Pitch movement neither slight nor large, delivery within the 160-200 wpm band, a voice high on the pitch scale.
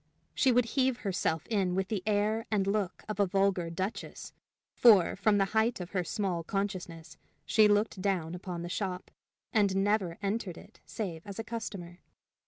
Yes: average, 3.0 semitones; average, 175 wpm; high, 195 Hz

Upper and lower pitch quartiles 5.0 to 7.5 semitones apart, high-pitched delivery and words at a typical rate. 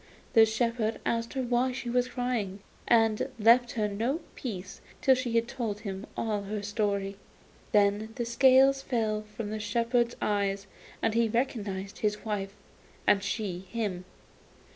No: average, 2.8 semitones; high, 220 Hz; average, 145 wpm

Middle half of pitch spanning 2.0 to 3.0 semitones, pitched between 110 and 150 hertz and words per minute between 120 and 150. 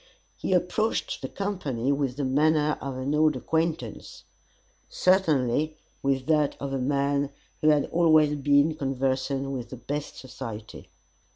Yes: narrow, 2.6 semitones; medium, 140 Hz; slow, 135 wpm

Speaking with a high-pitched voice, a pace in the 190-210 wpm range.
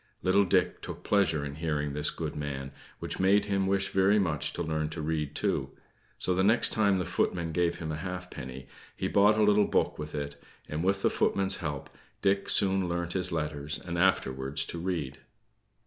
No: very low, 85 Hz; average, 195 wpm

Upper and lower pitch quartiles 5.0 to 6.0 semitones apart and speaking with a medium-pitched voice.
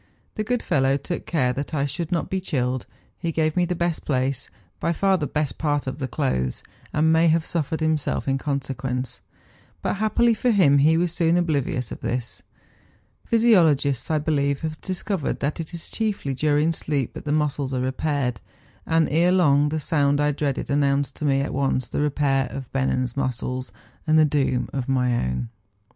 No: average, 3.3 semitones; medium, 145 Hz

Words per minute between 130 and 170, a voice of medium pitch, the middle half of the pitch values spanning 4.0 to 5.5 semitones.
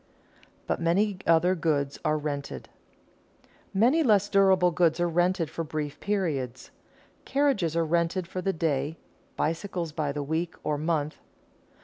No: average, 140 wpm; medium, 165 Hz; average, 3.6 semitones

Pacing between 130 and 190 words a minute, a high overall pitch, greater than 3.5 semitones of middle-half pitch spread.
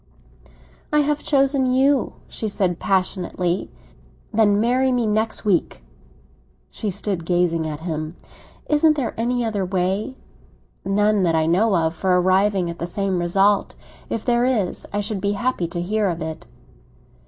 Yes: average, 155 wpm; high, 200 Hz; average, 4.4 semitones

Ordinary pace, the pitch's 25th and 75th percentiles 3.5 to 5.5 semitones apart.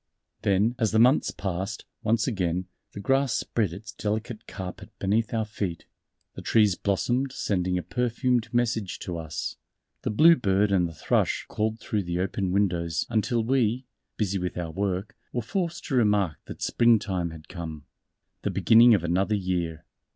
Yes: average, 165 wpm; average, 4.1 semitones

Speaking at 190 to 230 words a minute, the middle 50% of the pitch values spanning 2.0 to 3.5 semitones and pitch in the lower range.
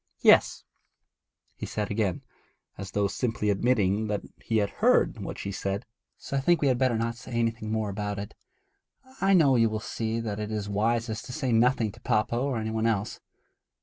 Yes: average, 195 wpm; narrow, 2.5 semitones; low, 110 Hz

